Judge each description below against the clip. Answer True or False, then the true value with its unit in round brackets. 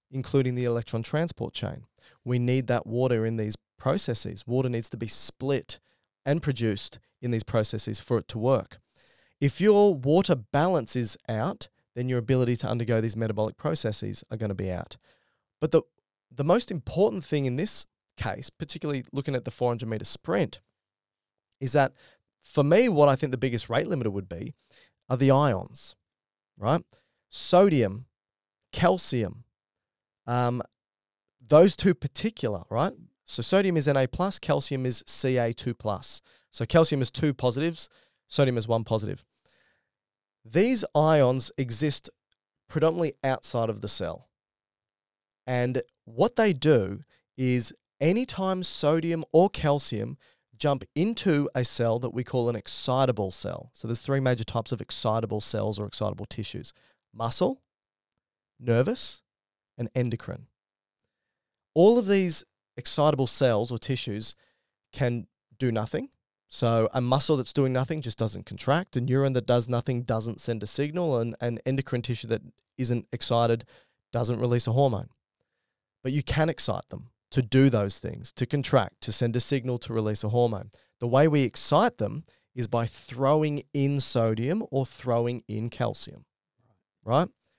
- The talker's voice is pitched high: False (125 Hz)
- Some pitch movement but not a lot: True (3.9 semitones)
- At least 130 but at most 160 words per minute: True (150 wpm)